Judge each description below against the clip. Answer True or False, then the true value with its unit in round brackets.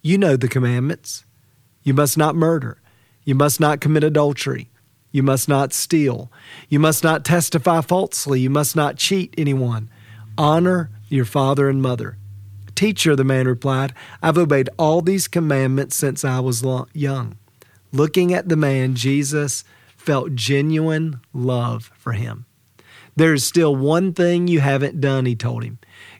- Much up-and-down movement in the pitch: False (4.0 semitones)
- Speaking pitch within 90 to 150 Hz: True (140 Hz)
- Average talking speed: True (150 wpm)